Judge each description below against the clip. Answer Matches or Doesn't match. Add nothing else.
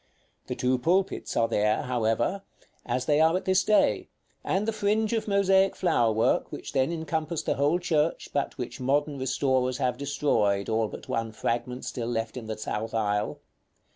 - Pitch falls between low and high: Doesn't match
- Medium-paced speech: Matches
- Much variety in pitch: Matches